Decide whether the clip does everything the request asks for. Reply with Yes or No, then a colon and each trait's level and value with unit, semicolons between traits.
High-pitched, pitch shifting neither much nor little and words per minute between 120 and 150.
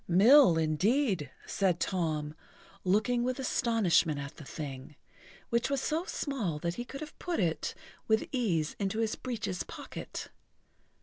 No: high, 200 Hz; wide, 7.3 semitones; average, 140 wpm